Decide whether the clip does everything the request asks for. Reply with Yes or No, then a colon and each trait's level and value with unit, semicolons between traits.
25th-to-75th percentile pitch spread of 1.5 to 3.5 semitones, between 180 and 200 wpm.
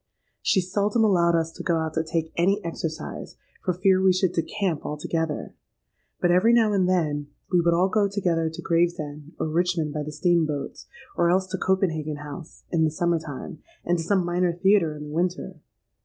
Yes: narrow, 2.6 semitones; average, 195 wpm